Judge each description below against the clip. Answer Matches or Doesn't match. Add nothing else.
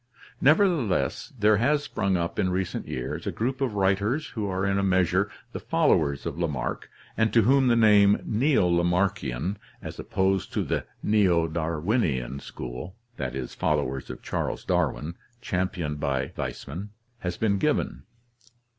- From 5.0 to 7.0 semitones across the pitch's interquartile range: Doesn't match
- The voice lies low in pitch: Matches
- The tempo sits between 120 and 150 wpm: Matches